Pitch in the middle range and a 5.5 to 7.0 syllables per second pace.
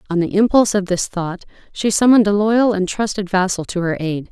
No: high, 195 Hz; 5.9 syllables/s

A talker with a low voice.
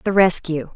No: medium, 175 Hz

